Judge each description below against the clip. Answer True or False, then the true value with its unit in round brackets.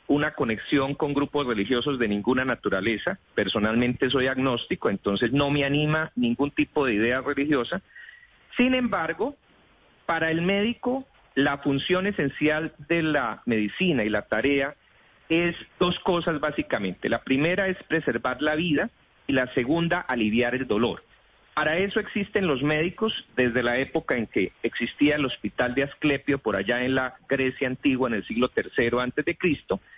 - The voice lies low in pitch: False (145 Hz)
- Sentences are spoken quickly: False (155 wpm)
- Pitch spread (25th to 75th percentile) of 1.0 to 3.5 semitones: False (4.3 semitones)